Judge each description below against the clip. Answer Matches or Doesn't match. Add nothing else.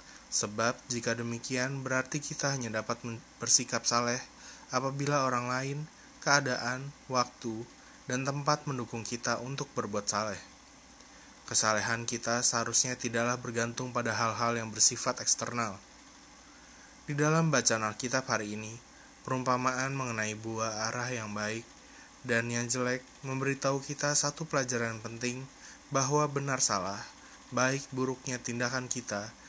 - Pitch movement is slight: Doesn't match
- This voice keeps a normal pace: Matches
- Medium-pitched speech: Doesn't match